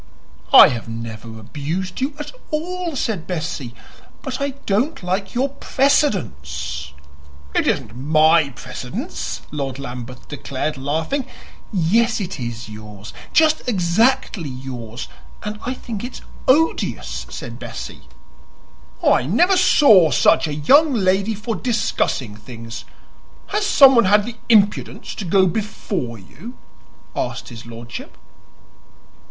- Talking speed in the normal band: No, slow, 120 wpm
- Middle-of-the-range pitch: Yes, medium, 180 Hz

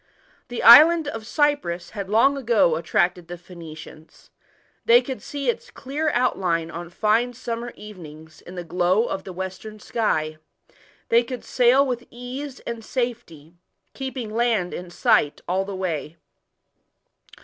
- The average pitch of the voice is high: Yes, high, 215 Hz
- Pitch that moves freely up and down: Yes, wide, 6.0 semitones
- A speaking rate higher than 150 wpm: No, average, 140 wpm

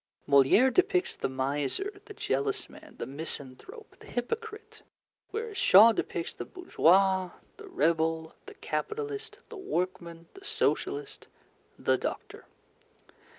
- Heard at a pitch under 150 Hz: No, very high, 250 Hz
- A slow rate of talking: Yes, slow, 115 wpm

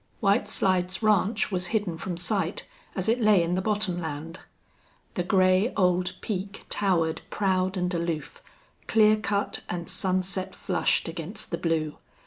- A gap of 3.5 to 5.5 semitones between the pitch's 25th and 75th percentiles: No, average, 2.7 semitones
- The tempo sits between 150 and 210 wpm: No, average, 140 wpm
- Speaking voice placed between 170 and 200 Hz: Yes, medium, 185 Hz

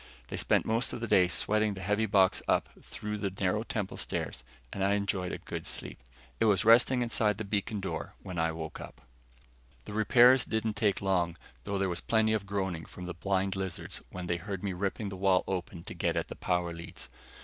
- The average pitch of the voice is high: No, low, 100 Hz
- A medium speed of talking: No, fast, 215 wpm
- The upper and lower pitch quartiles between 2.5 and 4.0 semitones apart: Yes, average, 2.9 semitones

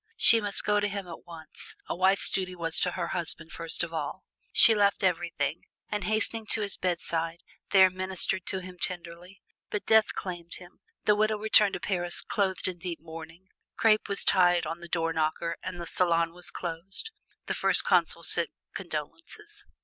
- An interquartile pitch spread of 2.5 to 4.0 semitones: Yes, average, 2.9 semitones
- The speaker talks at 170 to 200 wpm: Yes, average, 180 wpm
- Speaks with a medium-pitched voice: Yes, medium, 180 Hz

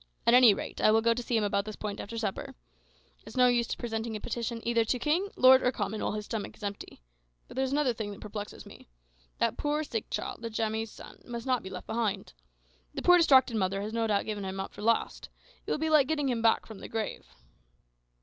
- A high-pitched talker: Yes, high, 225 Hz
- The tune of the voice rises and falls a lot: No, average, 3.0 semitones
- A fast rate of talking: Yes, fast, 240 wpm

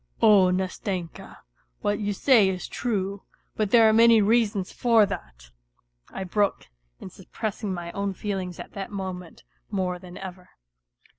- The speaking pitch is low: No, high, 195 Hz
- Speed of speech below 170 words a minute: Yes, average, 150 wpm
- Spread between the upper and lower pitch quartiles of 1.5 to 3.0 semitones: Yes, narrow, 2.6 semitones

